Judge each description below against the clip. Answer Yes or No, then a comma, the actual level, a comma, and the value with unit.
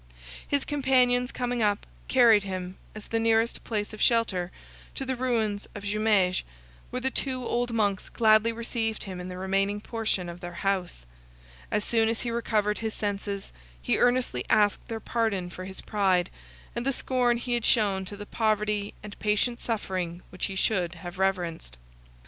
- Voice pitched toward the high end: Yes, high, 210 Hz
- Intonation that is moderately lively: Yes, average, 3.5 semitones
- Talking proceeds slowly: No, average, 170 wpm